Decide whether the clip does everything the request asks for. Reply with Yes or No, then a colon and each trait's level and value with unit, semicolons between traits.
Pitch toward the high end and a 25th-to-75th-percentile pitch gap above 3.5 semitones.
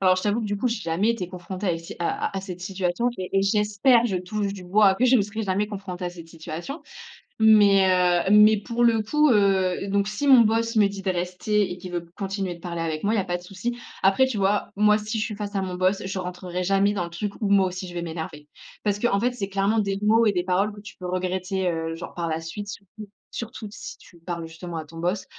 No: high, 195 Hz; average, 2.7 semitones